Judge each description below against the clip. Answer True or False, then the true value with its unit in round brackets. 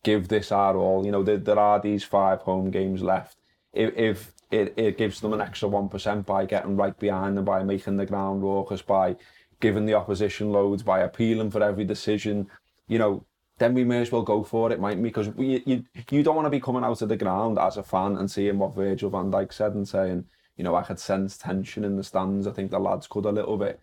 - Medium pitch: False (100 Hz)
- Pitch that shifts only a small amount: True (1.7 semitones)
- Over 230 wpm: True (245 wpm)